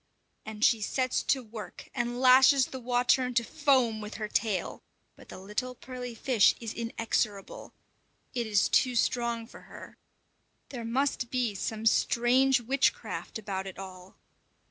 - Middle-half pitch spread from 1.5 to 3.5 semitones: Yes, average, 2.8 semitones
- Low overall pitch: No, high, 235 Hz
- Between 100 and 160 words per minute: Yes, average, 150 wpm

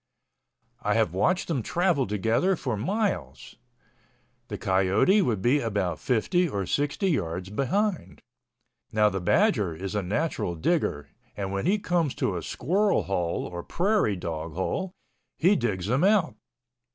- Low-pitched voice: Yes, low, 120 Hz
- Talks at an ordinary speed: Yes, average, 145 wpm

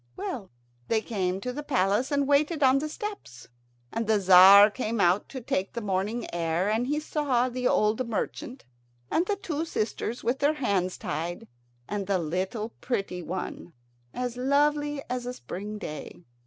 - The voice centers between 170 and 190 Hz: No, high, 230 Hz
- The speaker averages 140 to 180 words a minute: Yes, average, 170 wpm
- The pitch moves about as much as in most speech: No, wide, 6.2 semitones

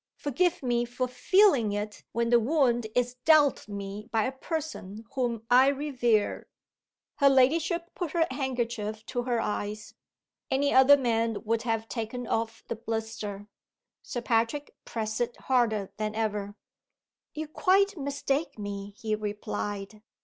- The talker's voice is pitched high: Yes, high, 235 Hz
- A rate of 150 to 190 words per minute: No, average, 140 wpm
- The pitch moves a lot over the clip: No, average, 4.0 semitones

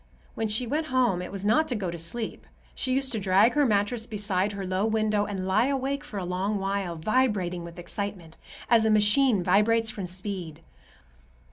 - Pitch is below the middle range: No, high, 205 Hz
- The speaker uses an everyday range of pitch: Yes, average, 3.7 semitones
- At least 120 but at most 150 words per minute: No, average, 195 wpm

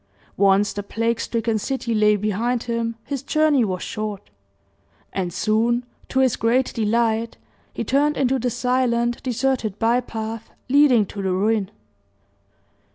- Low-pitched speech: No, high, 230 Hz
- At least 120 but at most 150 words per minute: Yes, average, 140 wpm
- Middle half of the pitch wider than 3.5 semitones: No, average, 2.8 semitones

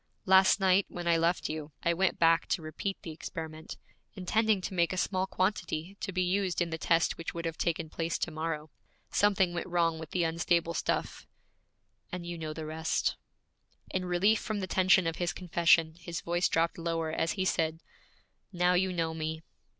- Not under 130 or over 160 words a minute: No, average, 190 wpm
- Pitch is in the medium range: Yes, medium, 170 Hz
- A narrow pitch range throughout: Yes, narrow, 2.2 semitones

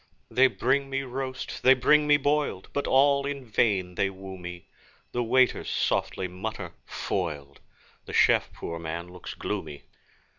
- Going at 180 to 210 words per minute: No, average, 150 wpm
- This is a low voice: Yes, low, 120 Hz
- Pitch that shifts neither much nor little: No, wide, 7.1 semitones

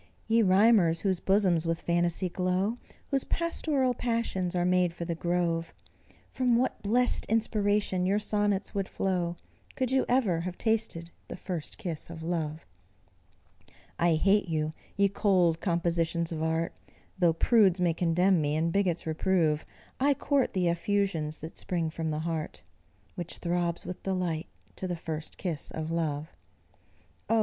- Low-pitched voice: No, medium, 180 Hz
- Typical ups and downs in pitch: Yes, average, 3.4 semitones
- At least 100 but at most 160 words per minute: Yes, average, 150 wpm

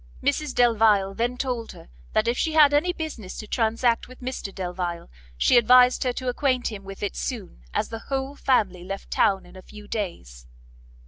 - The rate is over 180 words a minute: Yes, average, 190 wpm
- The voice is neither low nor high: No, high, 230 Hz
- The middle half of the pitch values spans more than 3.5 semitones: Yes, average, 4.6 semitones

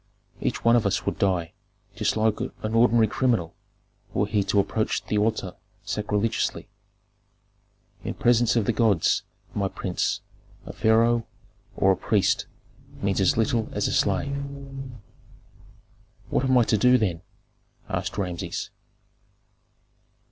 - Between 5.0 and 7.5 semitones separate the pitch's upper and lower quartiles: No, average, 2.8 semitones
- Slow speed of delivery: Yes, slow, 130 wpm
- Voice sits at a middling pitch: No, low, 110 Hz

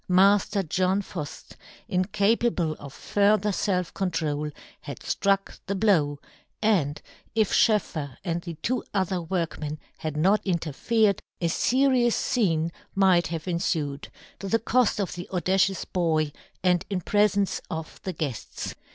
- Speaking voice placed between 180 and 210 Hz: Yes, medium, 185 Hz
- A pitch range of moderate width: Yes, average, 3.9 semitones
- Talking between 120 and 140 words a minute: Yes, slow, 135 wpm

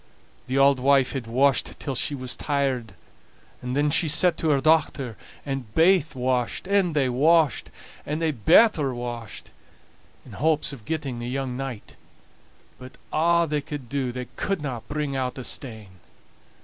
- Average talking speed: Yes, average, 160 wpm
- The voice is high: No, low, 135 Hz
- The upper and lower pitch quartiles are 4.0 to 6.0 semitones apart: No, average, 3.3 semitones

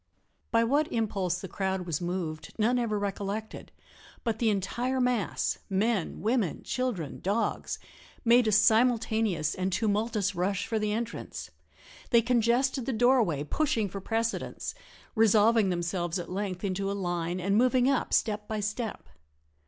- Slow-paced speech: No, average, 145 wpm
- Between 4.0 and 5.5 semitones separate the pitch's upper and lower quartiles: No, average, 3.6 semitones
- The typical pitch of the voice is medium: No, high, 215 Hz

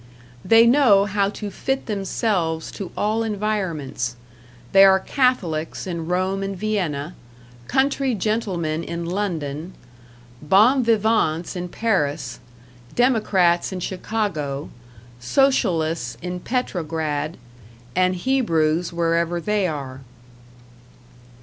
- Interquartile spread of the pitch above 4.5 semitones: Yes, average, 4.9 semitones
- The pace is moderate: No, slow, 100 wpm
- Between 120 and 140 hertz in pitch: No, medium, 185 Hz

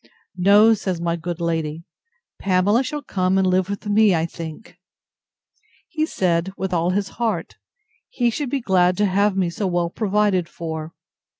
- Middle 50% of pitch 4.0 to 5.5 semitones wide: No, average, 3.5 semitones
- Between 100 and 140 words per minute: No, average, 165 wpm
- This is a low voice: No, medium, 185 Hz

